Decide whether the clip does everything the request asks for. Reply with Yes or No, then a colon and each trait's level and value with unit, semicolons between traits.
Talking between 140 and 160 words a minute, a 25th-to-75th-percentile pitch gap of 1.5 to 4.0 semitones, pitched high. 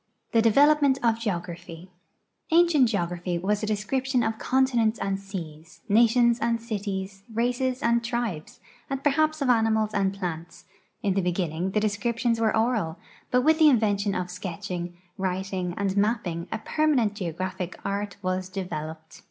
No: average, 150 wpm; average, 4.5 semitones; high, 205 Hz